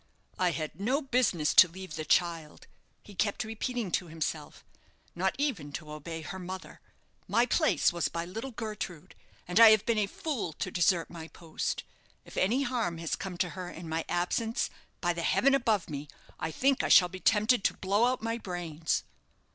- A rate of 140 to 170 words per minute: No, average, 185 wpm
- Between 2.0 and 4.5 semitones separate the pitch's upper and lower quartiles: No, average, 5.2 semitones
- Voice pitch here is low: No, medium, 185 Hz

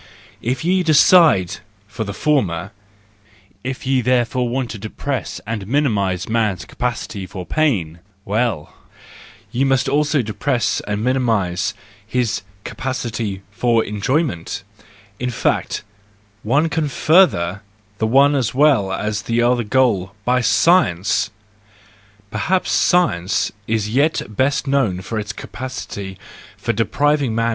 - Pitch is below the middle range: Yes, low, 120 Hz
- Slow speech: Yes, slow, 125 wpm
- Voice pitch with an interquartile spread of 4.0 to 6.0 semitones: Yes, average, 4.7 semitones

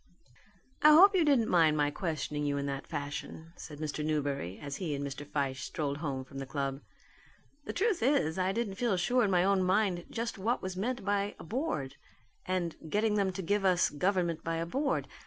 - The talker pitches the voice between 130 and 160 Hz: No, medium, 175 Hz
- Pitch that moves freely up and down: Yes, wide, 6.0 semitones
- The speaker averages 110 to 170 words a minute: No, fast, 205 wpm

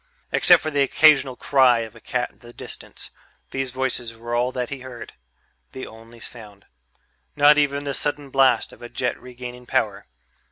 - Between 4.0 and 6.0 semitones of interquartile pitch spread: No, narrow, 2.6 semitones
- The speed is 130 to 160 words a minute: No, average, 175 wpm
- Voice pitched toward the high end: No, low, 125 Hz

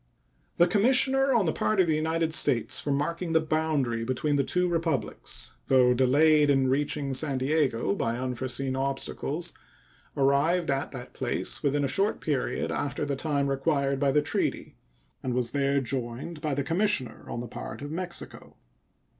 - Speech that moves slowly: No, average, 165 wpm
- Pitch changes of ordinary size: Yes, average, 3.4 semitones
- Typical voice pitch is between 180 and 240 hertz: No, medium, 140 Hz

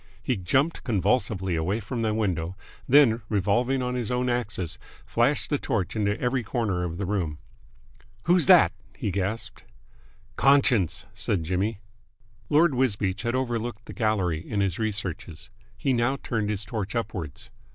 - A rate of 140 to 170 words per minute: Yes, average, 150 wpm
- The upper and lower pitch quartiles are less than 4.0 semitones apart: No, average, 4.4 semitones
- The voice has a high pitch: No, low, 110 Hz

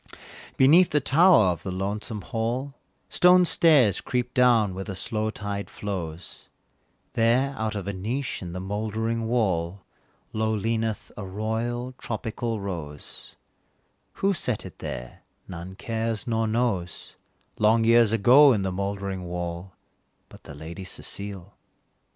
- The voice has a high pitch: No, low, 110 Hz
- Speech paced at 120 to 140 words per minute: Yes, slow, 135 wpm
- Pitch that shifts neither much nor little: Yes, average, 3.8 semitones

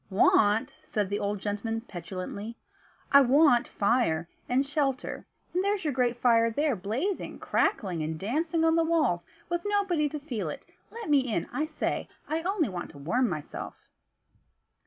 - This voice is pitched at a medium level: No, high, 245 Hz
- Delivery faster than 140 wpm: Yes, average, 160 wpm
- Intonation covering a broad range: Yes, wide, 7.4 semitones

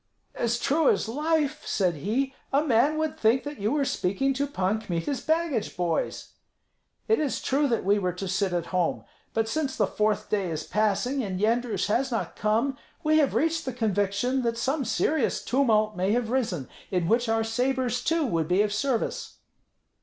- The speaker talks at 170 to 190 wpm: Yes, average, 185 wpm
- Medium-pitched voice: No, high, 230 Hz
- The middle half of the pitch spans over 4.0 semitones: Yes, average, 5.2 semitones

